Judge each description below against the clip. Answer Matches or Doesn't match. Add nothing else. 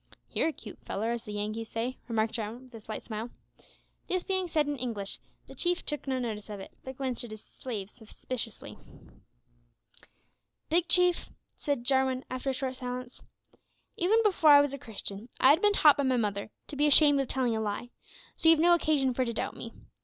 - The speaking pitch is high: Matches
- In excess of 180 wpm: Matches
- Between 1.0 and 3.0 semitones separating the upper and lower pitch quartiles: Doesn't match